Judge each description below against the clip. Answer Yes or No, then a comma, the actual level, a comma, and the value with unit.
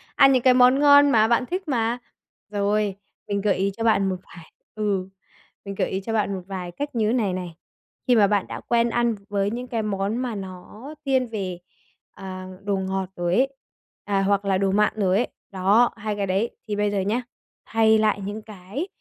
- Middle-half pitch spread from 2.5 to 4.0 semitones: Yes, average, 3.4 semitones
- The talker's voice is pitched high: Yes, high, 210 Hz